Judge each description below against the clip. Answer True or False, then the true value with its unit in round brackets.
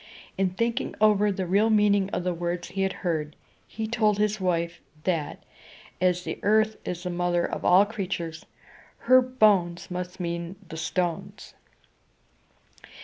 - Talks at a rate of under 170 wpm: True (145 wpm)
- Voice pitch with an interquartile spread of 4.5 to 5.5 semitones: False (3.2 semitones)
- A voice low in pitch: False (185 Hz)